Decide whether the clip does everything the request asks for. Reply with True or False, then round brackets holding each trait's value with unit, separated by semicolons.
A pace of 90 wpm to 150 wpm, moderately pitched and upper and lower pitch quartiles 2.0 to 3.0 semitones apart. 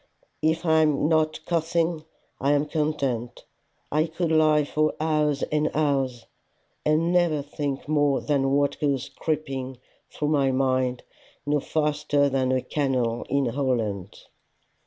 True (135 wpm; 145 Hz; 2.5 semitones)